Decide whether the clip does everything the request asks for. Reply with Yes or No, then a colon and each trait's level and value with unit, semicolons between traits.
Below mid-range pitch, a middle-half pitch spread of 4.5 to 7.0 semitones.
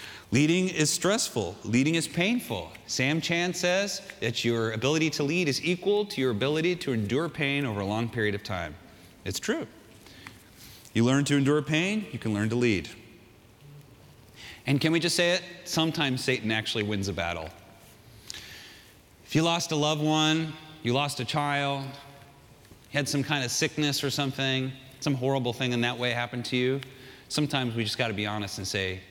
Yes: low, 130 Hz; wide, 5.4 semitones